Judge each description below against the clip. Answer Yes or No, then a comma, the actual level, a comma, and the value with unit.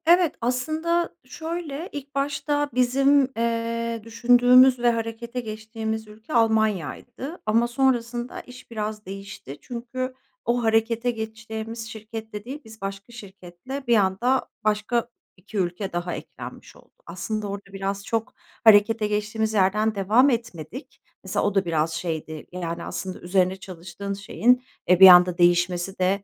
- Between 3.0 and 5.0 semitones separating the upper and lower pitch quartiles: Yes, average, 3.8 semitones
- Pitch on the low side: No, high, 220 Hz